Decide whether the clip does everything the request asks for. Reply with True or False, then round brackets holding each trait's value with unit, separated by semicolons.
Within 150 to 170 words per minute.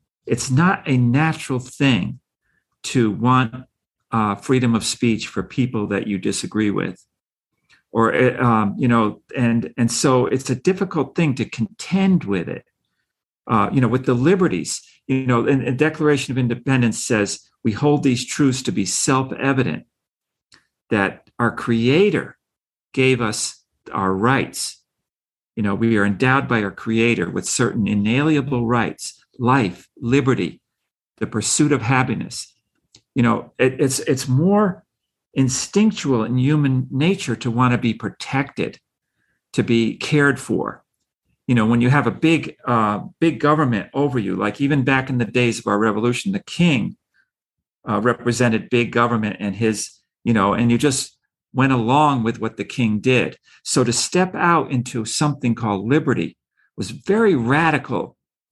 True (155 wpm)